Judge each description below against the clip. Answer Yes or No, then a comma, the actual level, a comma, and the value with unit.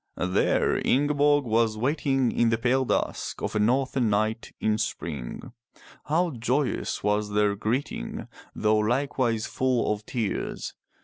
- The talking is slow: Yes, slow, 130 wpm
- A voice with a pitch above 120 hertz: No, low, 115 Hz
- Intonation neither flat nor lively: Yes, average, 3.8 semitones